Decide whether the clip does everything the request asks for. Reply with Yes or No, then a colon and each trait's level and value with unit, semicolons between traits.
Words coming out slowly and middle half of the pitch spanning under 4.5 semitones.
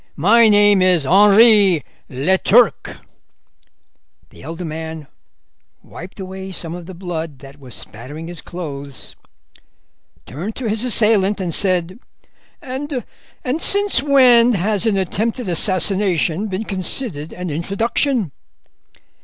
No: slow, 110 wpm; average, 4.8 semitones